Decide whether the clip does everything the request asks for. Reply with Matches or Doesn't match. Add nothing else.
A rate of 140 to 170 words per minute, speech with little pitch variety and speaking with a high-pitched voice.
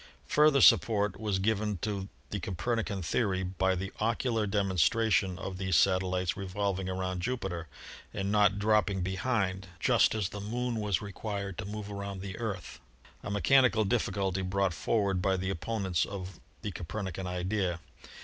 Doesn't match